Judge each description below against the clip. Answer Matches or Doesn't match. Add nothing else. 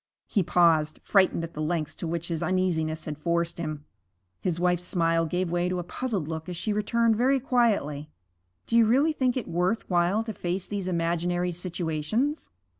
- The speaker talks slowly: Doesn't match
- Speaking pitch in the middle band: Matches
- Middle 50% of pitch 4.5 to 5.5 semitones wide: Doesn't match